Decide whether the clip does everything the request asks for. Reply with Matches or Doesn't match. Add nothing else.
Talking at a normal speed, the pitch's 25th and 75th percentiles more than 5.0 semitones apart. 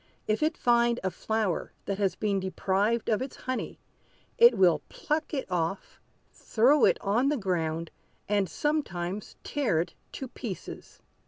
Matches